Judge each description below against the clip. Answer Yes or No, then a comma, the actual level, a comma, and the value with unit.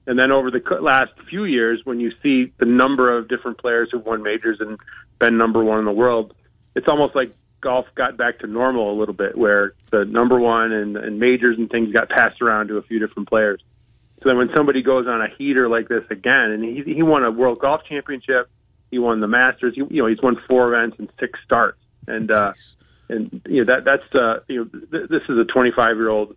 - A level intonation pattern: Yes, narrow, 2.3 semitones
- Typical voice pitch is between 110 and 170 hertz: Yes, low, 115 Hz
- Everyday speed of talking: No, fast, 230 wpm